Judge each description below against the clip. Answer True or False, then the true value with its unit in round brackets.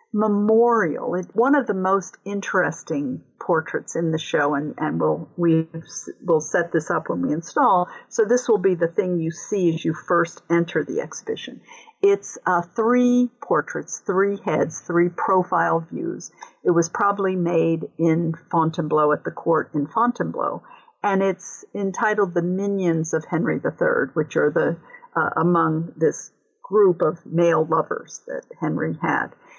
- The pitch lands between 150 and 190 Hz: True (185 Hz)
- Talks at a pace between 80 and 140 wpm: False (155 wpm)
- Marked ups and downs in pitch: True (6.1 semitones)